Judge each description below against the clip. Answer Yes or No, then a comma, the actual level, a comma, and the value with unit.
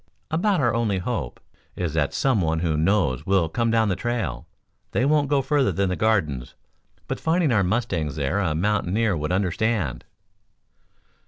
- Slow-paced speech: No, average, 165 wpm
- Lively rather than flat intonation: Yes, wide, 6.6 semitones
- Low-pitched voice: Yes, low, 100 Hz